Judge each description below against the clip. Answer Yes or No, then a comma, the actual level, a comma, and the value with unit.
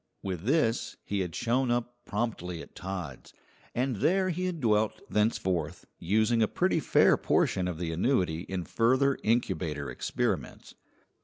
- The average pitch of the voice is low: Yes, low, 110 Hz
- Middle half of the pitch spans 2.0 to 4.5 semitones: No, average, 5.3 semitones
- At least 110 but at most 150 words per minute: Yes, average, 145 wpm